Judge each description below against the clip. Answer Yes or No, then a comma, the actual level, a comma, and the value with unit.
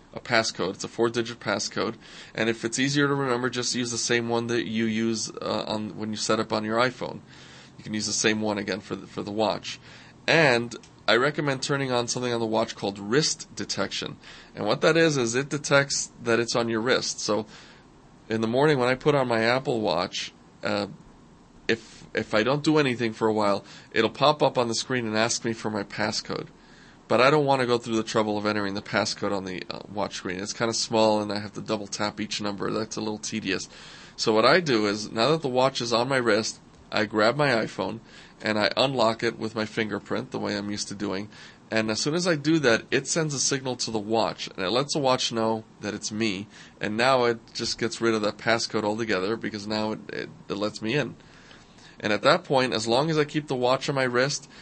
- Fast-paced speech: Yes, fast, 245 wpm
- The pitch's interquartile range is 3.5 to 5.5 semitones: No, average, 2.9 semitones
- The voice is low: Yes, low, 115 Hz